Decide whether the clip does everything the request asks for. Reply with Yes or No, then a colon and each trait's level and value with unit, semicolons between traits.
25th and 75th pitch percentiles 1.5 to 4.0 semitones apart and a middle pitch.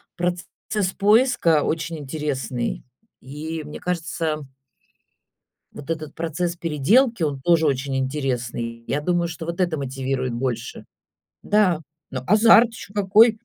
No: average, 4.9 semitones; medium, 160 Hz